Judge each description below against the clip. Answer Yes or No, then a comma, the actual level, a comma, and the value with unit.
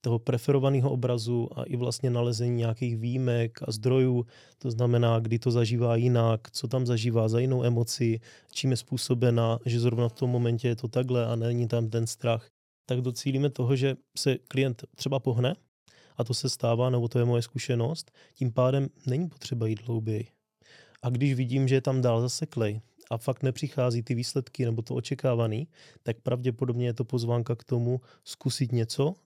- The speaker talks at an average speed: No, fast, 180 wpm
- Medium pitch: No, low, 125 Hz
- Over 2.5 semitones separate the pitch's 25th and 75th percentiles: No, narrow, 1.9 semitones